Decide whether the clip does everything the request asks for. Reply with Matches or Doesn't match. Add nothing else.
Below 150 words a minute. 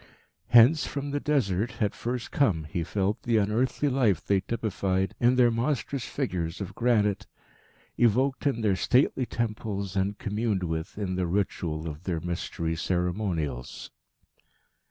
Matches